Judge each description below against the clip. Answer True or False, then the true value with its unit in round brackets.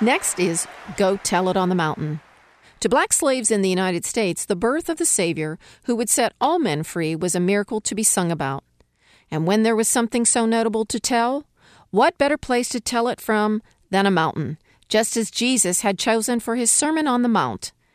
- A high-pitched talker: True (220 Hz)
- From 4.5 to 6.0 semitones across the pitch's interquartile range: True (5.0 semitones)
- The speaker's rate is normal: False (210 wpm)